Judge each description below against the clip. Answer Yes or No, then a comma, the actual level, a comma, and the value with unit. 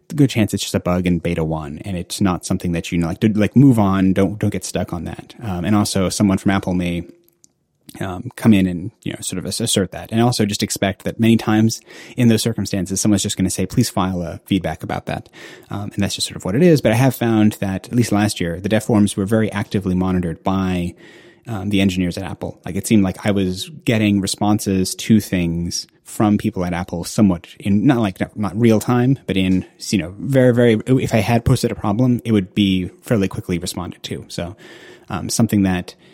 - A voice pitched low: Yes, low, 100 Hz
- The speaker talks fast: Yes, fast, 230 wpm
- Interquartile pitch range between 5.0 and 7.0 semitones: No, average, 3.2 semitones